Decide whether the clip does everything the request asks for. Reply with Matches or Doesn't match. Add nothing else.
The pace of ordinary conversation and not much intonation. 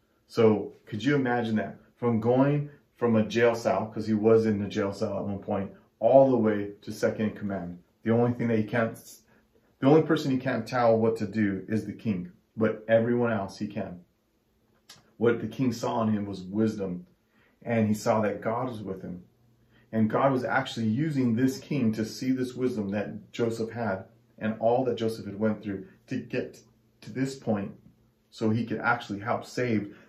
Matches